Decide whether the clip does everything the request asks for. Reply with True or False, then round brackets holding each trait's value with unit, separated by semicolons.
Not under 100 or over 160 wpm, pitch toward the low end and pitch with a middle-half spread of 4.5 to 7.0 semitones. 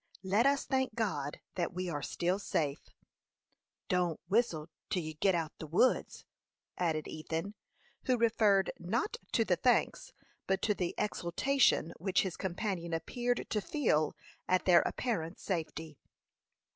False (145 wpm; 185 Hz; 5.0 semitones)